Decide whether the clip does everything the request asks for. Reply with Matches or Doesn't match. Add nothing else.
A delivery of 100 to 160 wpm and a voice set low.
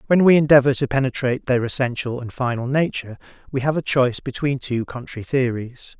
Doesn't match